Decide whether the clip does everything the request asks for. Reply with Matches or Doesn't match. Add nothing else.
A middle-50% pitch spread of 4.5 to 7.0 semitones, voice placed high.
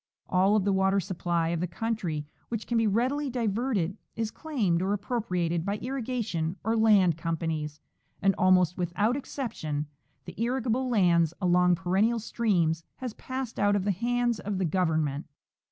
Matches